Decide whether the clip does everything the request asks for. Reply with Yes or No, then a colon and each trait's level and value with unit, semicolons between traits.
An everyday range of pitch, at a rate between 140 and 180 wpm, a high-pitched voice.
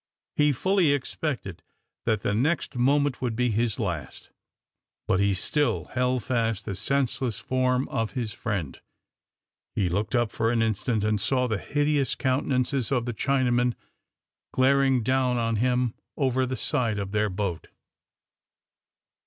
No: average, 3.4 semitones; average, 145 wpm; low, 125 Hz